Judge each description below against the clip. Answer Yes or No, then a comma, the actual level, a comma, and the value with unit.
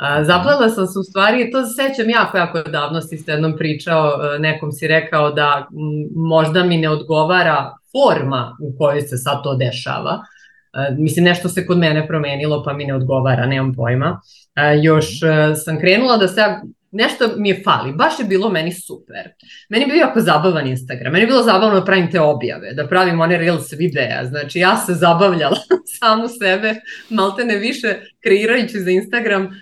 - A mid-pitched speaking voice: Yes, medium, 170 Hz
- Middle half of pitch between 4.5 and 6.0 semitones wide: Yes, average, 5.3 semitones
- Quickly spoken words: Yes, fast, 185 wpm